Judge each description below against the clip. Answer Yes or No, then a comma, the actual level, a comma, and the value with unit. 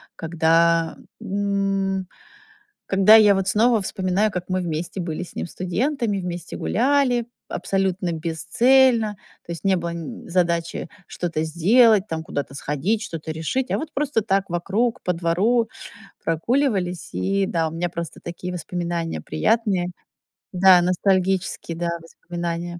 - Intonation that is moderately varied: Yes, average, 3.6 semitones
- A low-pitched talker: No, medium, 185 Hz